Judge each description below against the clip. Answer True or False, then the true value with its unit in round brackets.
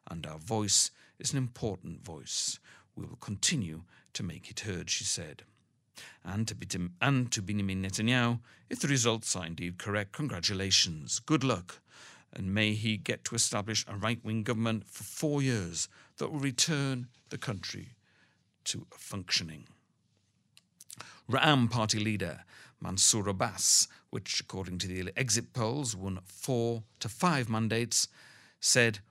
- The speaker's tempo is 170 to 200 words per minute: False (145 wpm)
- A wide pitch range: False (4.5 semitones)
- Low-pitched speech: True (110 Hz)